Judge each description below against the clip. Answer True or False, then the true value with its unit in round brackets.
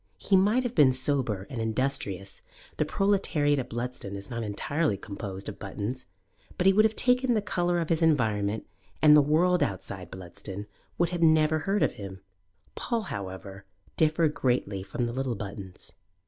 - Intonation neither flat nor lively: False (8.7 semitones)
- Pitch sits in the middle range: False (130 Hz)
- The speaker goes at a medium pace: True (170 wpm)